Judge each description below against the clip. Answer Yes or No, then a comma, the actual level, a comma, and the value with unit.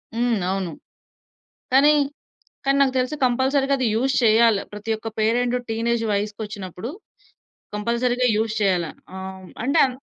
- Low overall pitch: No, high, 230 Hz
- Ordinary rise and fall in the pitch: Yes, average, 3.4 semitones